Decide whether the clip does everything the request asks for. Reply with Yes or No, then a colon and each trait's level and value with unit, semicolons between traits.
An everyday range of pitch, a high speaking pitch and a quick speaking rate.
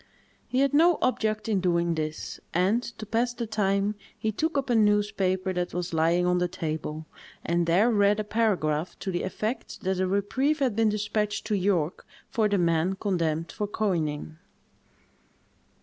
No: average, 4.0 semitones; high, 200 Hz; average, 170 wpm